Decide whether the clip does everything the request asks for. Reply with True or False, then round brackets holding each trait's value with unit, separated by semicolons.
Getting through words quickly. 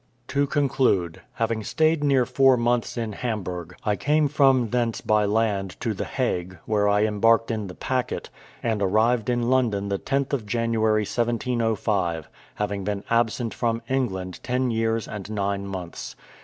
False (155 wpm)